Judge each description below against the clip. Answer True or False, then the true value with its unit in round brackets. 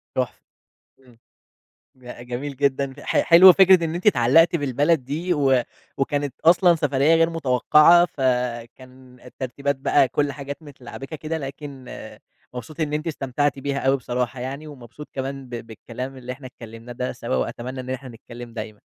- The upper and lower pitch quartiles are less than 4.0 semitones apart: True (3.0 semitones)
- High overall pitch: False (135 Hz)